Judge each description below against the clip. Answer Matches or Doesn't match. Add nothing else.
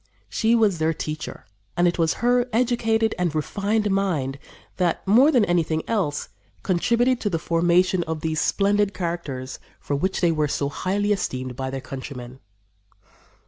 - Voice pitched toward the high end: Doesn't match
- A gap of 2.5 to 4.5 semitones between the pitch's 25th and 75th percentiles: Doesn't match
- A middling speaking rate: Matches